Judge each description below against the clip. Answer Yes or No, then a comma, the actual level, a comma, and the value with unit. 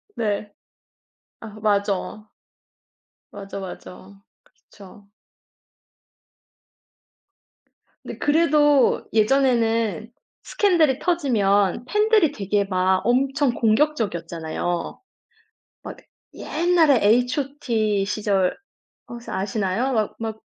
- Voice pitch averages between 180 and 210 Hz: No, high, 220 Hz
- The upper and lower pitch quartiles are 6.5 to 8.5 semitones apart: No, wide, 5.5 semitones